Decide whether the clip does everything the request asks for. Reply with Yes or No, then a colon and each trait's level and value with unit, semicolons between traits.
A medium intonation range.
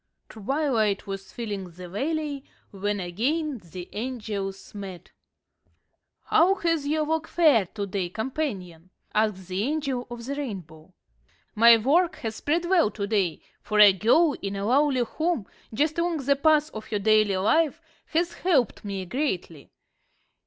No: wide, 7.3 semitones